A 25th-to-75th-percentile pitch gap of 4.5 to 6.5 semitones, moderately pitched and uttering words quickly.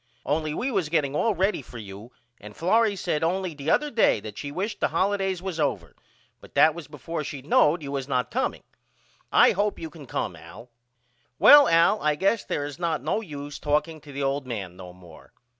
Yes: average, 5.2 semitones; medium, 150 Hz; fast, 210 wpm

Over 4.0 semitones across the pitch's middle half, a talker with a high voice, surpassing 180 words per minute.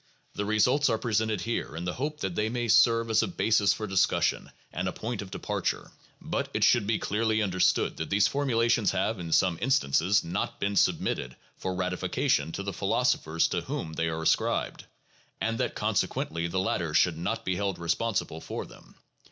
No: average, 4.5 semitones; low, 100 Hz; average, 190 wpm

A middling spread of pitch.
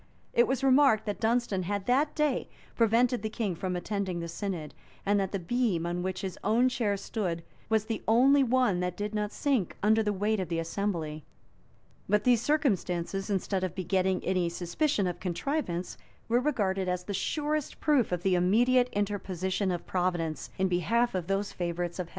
Yes: average, 4.7 semitones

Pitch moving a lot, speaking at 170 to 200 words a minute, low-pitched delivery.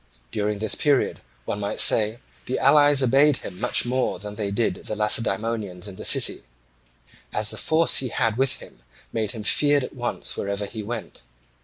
No: average, 3.9 semitones; average, 180 wpm; low, 115 Hz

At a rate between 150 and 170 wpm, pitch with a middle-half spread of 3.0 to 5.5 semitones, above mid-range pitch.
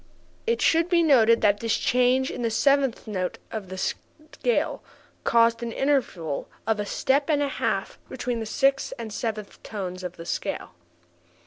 Yes: average, 165 wpm; average, 4.7 semitones; high, 230 Hz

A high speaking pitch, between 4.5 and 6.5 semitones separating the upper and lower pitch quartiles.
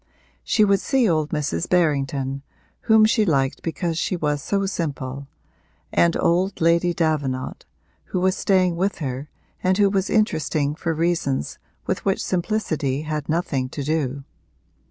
No: medium, 165 Hz; average, 4.8 semitones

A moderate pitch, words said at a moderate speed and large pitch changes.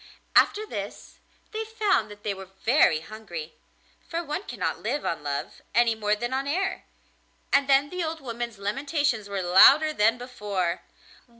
No: high, 240 Hz; average, 160 wpm; wide, 6.7 semitones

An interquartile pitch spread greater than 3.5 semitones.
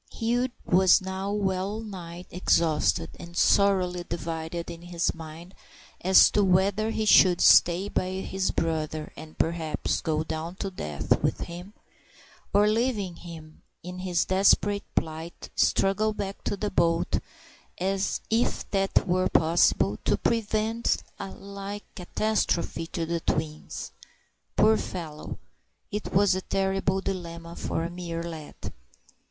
No: average, 3.1 semitones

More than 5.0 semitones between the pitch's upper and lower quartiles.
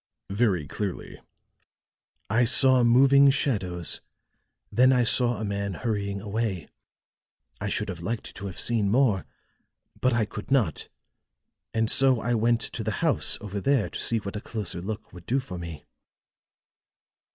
No: average, 3.7 semitones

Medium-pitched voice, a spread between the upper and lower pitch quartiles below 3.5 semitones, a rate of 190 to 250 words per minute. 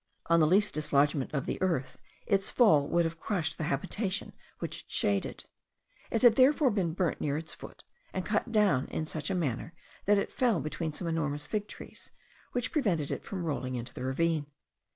No: medium, 165 Hz; wide, 5.4 semitones; average, 195 wpm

